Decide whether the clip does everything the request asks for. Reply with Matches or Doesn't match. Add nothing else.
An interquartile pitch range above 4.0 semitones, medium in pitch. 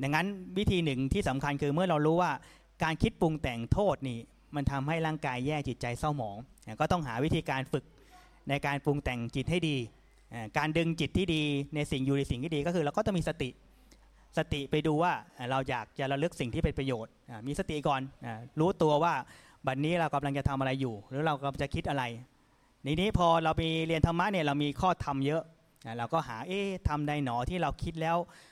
Doesn't match